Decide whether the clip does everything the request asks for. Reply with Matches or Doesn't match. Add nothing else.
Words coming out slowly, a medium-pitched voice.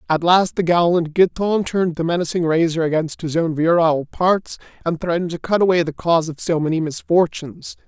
Doesn't match